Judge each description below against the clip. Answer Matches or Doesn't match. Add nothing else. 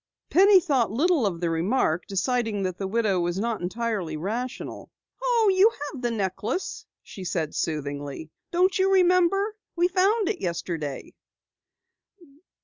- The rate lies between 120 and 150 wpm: Matches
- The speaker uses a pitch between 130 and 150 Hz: Doesn't match